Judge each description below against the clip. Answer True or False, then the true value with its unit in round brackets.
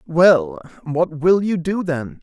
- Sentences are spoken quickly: False (160 wpm)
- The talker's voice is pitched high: False (165 Hz)